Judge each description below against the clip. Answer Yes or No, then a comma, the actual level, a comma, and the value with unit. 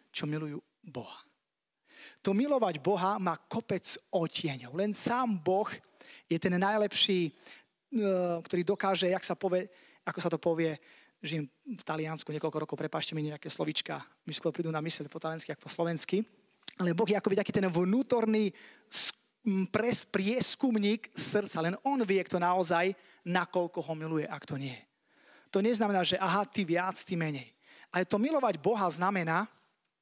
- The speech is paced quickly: No, average, 155 wpm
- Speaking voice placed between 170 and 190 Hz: Yes, medium, 185 Hz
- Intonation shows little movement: No, average, 4.0 semitones